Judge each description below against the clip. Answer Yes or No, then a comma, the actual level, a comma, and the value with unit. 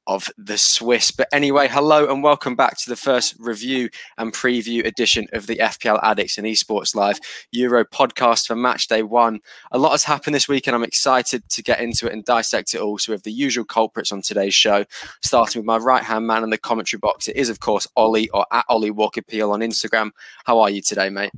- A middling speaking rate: No, fast, 230 wpm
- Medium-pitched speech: No, low, 115 Hz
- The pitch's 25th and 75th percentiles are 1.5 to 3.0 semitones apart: Yes, narrow, 2.4 semitones